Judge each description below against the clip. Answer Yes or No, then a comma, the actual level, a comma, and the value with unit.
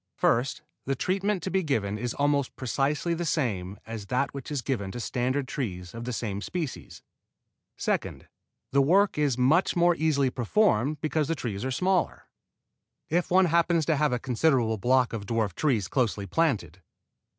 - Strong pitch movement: Yes, wide, 5.7 semitones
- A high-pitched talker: No, low, 135 Hz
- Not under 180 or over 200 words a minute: No, average, 170 wpm